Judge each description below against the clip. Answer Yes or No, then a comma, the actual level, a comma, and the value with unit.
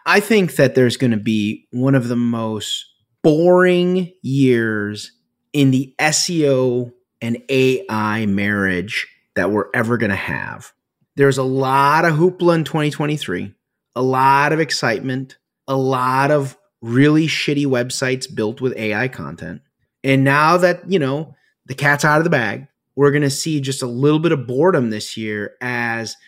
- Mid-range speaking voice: No, low, 130 Hz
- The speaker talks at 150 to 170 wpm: Yes, average, 160 wpm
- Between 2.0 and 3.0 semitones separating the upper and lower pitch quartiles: No, average, 4.2 semitones